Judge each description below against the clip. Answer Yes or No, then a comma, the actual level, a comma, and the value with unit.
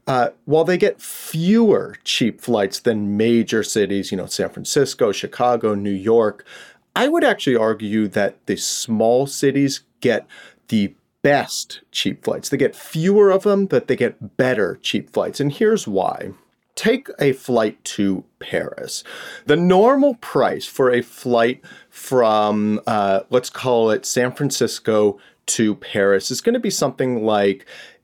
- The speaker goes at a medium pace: Yes, average, 150 wpm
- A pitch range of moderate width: No, wide, 8.9 semitones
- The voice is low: Yes, low, 125 Hz